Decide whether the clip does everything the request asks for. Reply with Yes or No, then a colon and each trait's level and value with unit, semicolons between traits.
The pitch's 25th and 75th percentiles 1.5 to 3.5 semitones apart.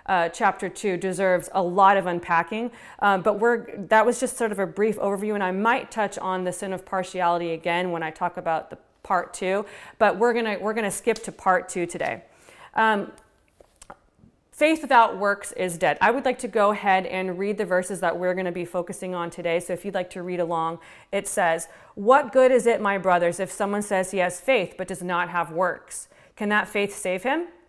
Yes: average, 3.1 semitones